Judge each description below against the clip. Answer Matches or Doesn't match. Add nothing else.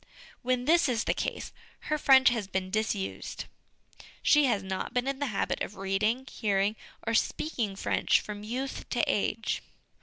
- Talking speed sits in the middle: Matches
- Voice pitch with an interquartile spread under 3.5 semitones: Doesn't match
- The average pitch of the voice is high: Matches